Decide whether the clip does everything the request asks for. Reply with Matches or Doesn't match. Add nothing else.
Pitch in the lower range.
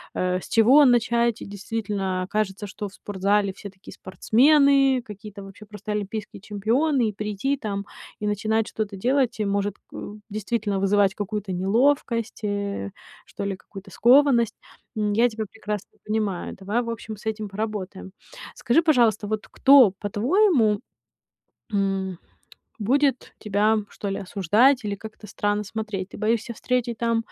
Doesn't match